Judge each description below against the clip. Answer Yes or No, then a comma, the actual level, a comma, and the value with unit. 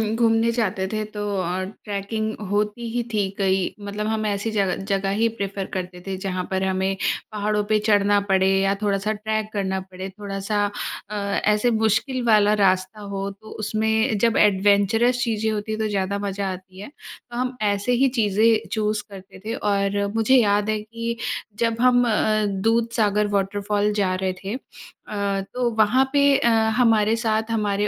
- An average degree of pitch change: No, narrow, 2.1 semitones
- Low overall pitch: No, high, 210 Hz